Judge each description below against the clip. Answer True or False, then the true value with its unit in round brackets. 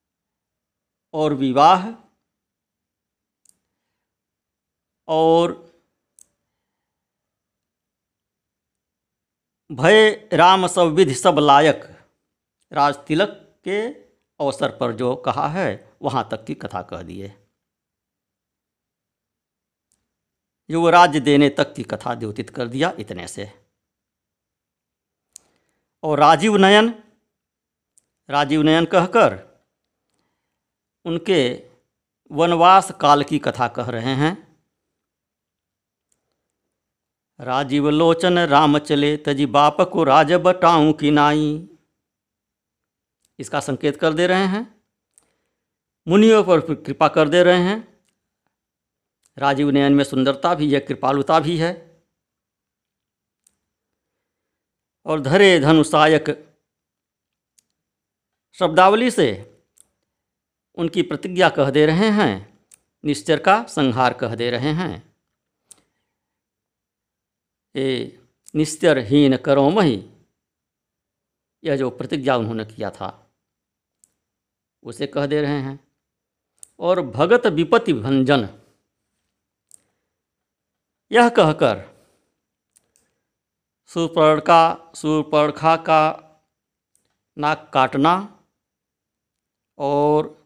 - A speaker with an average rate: False (85 wpm)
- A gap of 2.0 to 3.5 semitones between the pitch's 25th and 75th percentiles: False (4.2 semitones)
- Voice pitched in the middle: True (150 Hz)